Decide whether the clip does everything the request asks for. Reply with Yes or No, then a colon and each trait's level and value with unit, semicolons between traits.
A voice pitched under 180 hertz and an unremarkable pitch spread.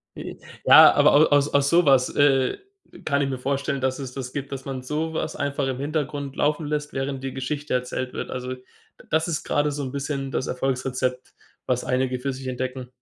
No: low, 135 Hz; narrow, 2.0 semitones